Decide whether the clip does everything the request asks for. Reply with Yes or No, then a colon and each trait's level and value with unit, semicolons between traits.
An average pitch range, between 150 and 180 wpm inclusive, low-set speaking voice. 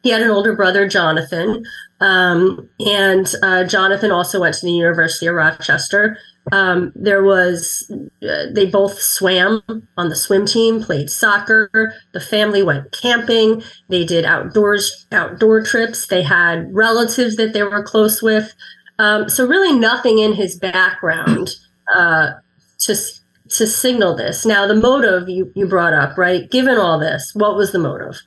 No: average, 3.4 semitones; average, 155 wpm; high, 205 Hz